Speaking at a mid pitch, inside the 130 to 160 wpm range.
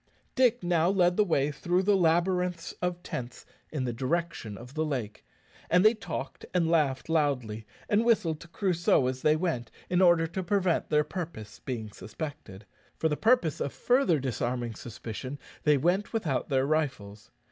No: medium, 160 Hz; average, 170 wpm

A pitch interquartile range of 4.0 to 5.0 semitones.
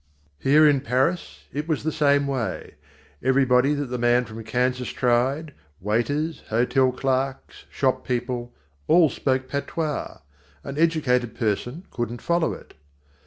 No: average, 3.0 semitones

